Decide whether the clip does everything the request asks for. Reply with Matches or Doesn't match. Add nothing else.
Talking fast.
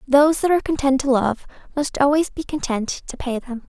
Matches